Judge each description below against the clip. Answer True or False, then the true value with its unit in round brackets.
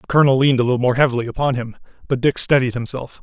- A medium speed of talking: False (240 wpm)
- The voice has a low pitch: True (130 Hz)